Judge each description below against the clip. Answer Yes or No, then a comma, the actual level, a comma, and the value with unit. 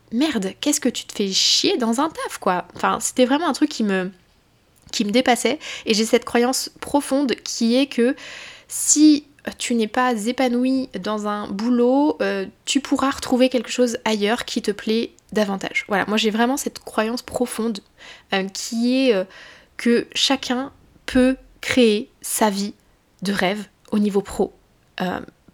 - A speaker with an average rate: Yes, average, 165 wpm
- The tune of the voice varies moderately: Yes, average, 3.5 semitones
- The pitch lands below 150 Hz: No, high, 240 Hz